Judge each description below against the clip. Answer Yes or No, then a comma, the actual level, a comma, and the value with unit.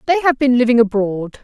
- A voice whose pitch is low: No, high, 245 Hz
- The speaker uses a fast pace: Yes, fast, 210 wpm